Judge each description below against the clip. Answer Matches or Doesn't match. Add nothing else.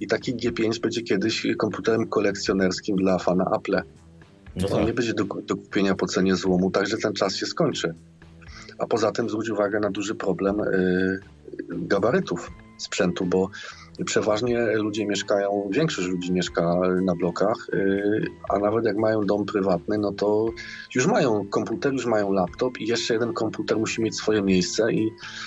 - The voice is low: Matches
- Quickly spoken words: Matches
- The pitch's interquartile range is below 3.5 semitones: Matches